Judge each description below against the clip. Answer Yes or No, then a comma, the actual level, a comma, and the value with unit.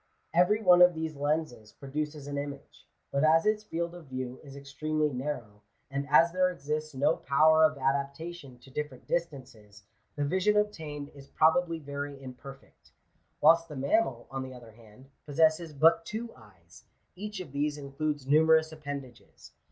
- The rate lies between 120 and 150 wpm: No, average, 160 wpm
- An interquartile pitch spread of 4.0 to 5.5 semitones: No, average, 3.1 semitones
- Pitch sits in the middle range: Yes, medium, 145 Hz